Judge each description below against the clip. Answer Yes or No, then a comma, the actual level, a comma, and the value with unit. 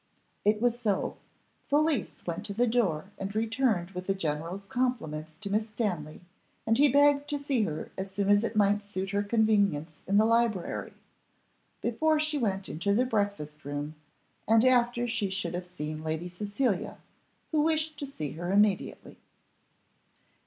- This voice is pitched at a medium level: No, high, 205 Hz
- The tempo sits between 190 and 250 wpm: No, average, 160 wpm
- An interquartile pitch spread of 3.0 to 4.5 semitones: No, average, 5.1 semitones